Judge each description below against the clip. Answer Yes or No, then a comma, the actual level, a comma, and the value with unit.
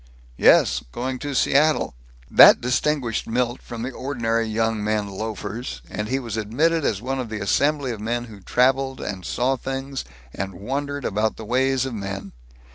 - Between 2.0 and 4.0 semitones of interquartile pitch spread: Yes, average, 3.7 semitones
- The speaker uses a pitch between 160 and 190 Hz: No, low, 120 Hz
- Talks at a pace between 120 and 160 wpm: No, average, 170 wpm